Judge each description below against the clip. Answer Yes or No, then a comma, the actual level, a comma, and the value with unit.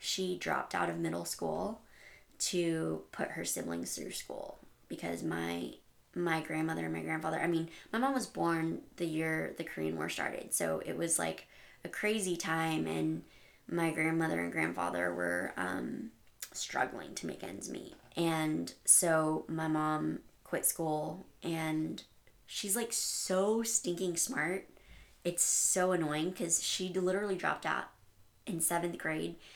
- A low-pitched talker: No, medium, 160 Hz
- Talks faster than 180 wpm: No, average, 150 wpm